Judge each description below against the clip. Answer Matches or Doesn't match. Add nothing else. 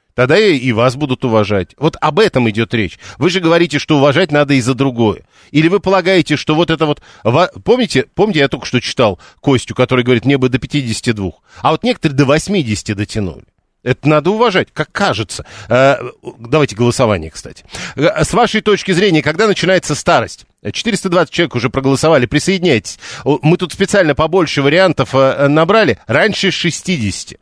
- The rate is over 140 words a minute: Matches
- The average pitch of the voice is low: Doesn't match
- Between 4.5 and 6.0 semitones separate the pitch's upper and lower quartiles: Matches